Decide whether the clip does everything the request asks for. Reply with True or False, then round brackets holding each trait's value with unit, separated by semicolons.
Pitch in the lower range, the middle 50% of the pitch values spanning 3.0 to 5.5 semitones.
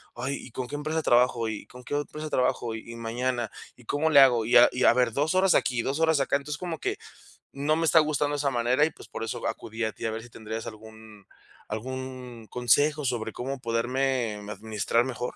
True (125 Hz; 4.1 semitones)